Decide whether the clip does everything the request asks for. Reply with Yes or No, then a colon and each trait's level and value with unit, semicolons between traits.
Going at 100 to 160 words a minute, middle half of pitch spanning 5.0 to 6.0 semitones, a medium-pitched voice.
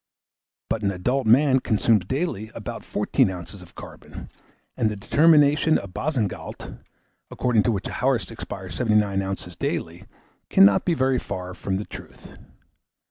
No: average, 145 wpm; wide, 5.4 semitones; low, 105 Hz